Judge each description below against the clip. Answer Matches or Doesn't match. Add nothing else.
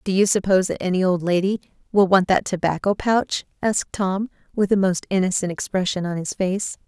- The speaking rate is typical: Matches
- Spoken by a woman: Matches